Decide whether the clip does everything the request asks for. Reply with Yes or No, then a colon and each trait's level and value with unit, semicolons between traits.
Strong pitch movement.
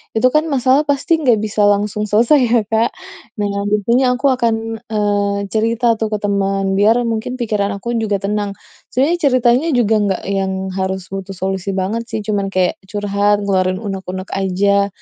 No: average, 3.0 semitones